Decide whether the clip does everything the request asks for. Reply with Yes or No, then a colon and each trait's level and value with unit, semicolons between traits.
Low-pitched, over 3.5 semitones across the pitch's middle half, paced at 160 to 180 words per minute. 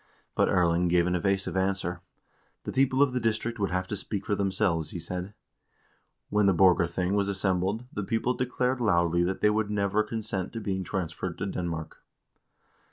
No: very low, 95 Hz; average, 3.0 semitones; average, 175 wpm